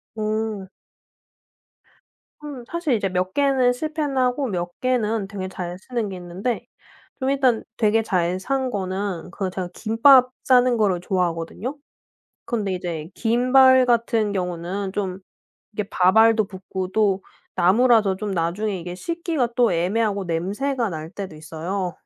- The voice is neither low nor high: No, high, 205 Hz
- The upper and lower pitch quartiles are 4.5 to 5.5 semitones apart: Yes, average, 5.1 semitones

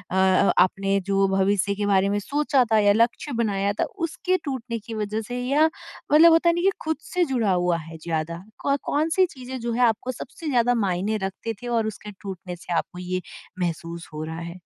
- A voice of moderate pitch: No, high, 210 Hz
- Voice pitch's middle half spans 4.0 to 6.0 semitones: Yes, wide, 5.5 semitones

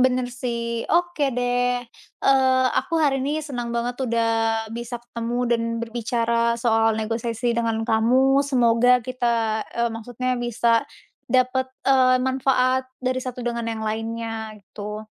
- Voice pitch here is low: No, high, 240 Hz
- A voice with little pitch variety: Yes, narrow, 1.9 semitones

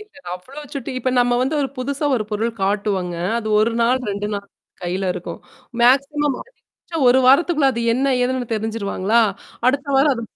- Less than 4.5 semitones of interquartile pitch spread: No, average, 4.8 semitones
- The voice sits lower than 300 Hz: Yes, high, 245 Hz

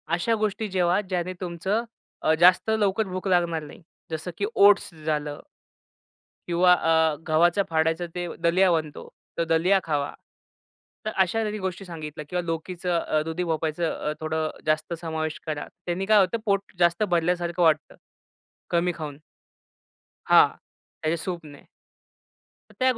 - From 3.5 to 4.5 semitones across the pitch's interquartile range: No, average, 2.8 semitones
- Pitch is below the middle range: No, medium, 175 Hz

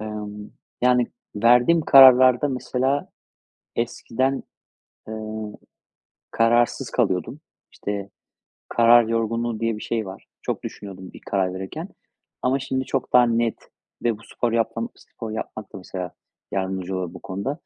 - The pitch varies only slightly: No, average, 3.7 semitones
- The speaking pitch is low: Yes, low, 115 Hz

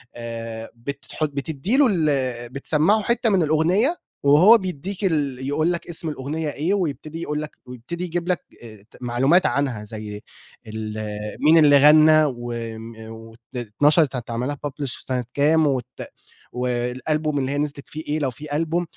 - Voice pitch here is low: No, medium, 145 Hz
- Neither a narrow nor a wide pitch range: Yes, average, 4.5 semitones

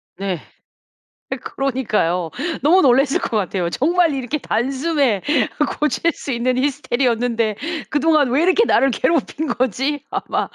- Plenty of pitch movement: No, average, 4.1 semitones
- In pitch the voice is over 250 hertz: Yes, very high, 265 Hz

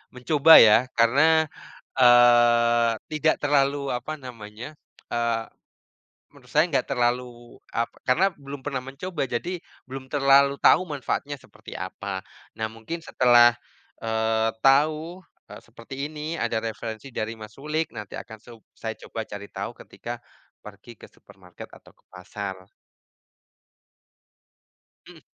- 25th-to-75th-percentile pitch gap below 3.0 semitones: No, average, 4.1 semitones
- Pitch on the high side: No, low, 125 Hz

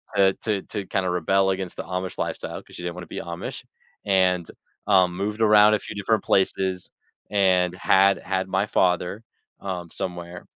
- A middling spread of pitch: No, narrow, 1.7 semitones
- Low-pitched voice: Yes, very low, 95 Hz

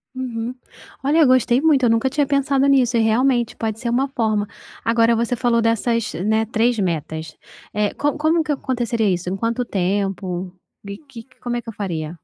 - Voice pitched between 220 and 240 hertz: Yes, high, 230 Hz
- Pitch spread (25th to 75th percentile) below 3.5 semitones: No, average, 3.9 semitones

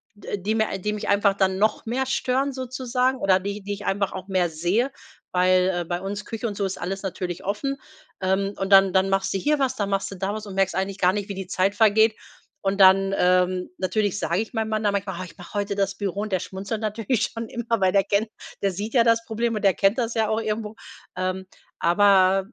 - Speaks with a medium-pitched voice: No, high, 200 Hz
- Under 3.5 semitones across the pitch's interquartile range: Yes, narrow, 2.4 semitones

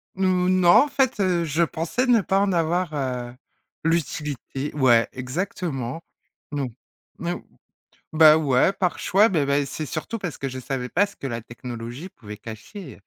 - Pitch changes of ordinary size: No, wide, 6.1 semitones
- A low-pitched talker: No, medium, 155 Hz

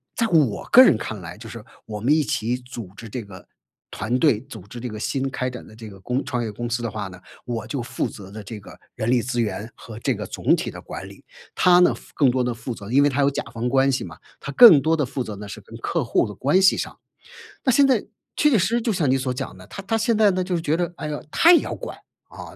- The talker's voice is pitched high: No, low, 125 Hz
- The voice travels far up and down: Yes, wide, 6.1 semitones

